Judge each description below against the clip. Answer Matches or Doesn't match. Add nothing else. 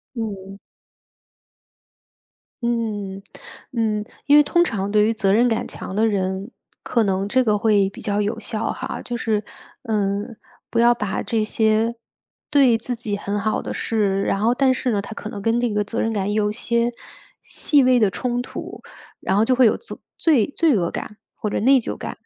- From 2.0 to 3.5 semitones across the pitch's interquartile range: Matches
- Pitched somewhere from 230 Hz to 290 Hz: Doesn't match